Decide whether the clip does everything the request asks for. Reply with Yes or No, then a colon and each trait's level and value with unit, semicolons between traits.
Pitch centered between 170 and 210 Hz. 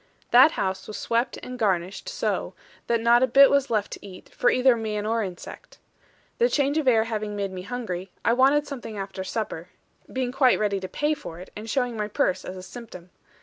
No: high, 225 Hz